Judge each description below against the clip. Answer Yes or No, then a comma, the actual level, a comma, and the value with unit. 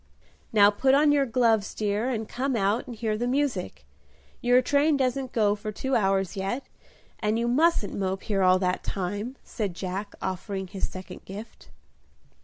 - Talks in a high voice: Yes, high, 215 Hz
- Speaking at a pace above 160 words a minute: Yes, average, 170 wpm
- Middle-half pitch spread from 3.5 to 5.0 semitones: Yes, average, 4.4 semitones